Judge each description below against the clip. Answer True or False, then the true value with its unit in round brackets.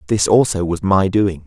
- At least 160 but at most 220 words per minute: True (205 wpm)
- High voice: False (95 Hz)